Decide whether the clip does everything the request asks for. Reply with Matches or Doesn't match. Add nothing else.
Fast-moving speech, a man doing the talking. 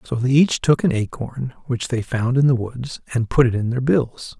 Matches